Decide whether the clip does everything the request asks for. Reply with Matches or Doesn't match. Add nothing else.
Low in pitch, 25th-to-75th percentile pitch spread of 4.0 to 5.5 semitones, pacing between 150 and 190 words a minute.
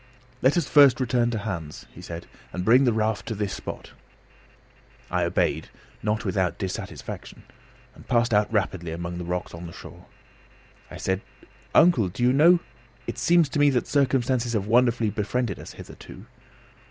Matches